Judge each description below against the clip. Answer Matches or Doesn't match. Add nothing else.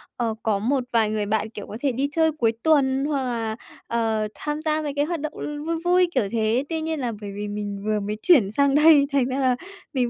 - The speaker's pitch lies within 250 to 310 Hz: Matches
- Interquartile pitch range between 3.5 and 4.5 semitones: Doesn't match